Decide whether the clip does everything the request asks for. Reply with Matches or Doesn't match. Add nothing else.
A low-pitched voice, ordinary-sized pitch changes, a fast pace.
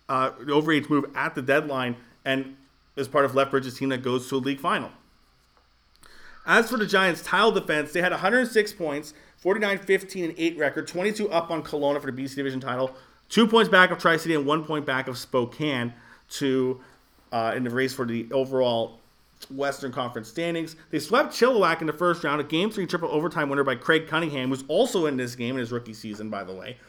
Doesn't match